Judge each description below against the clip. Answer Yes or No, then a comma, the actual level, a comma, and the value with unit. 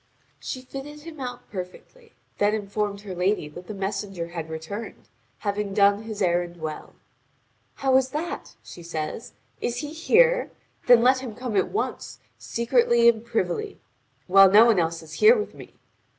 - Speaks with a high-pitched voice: Yes, high, 210 Hz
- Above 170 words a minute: No, average, 160 wpm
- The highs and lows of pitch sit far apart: Yes, wide, 5.9 semitones